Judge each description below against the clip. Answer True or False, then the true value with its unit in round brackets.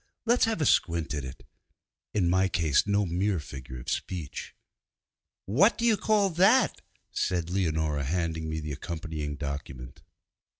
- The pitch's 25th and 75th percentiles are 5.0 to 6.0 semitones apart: True (5.6 semitones)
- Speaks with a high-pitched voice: False (85 Hz)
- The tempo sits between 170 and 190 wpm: False (145 wpm)